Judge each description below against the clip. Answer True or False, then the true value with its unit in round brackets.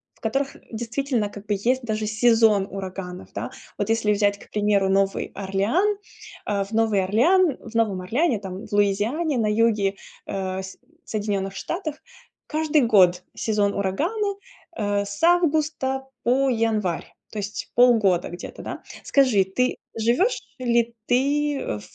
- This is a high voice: True (220 Hz)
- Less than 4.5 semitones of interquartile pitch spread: False (5.0 semitones)